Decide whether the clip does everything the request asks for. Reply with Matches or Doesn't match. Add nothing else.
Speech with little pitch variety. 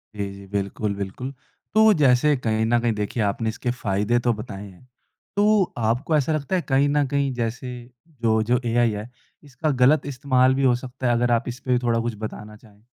Doesn't match